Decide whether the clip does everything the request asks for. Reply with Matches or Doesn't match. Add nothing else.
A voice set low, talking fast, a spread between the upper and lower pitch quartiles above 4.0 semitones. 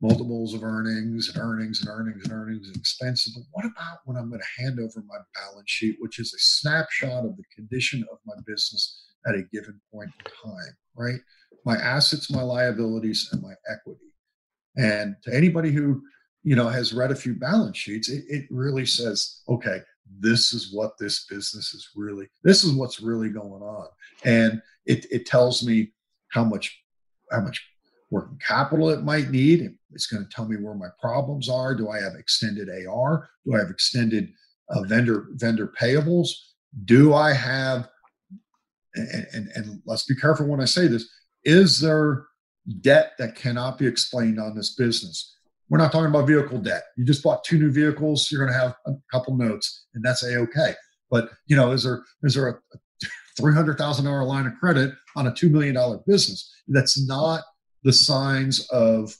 Doesn't match